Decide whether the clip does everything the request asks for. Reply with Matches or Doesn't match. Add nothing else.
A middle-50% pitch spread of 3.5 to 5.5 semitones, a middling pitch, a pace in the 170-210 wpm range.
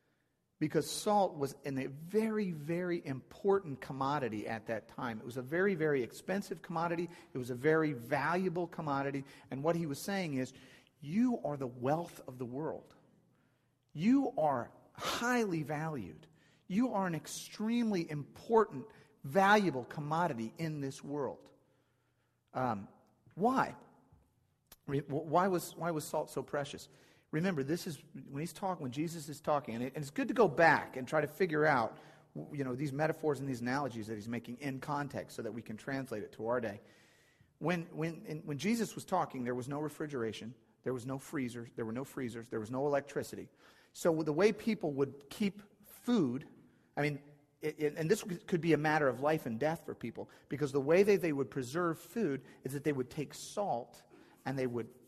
Matches